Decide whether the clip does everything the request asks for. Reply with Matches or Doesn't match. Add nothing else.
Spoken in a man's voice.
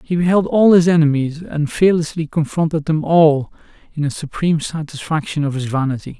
Matches